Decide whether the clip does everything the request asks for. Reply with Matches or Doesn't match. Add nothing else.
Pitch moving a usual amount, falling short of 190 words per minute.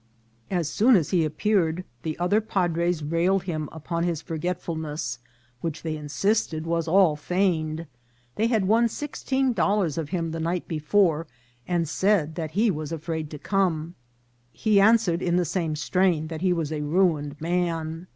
Matches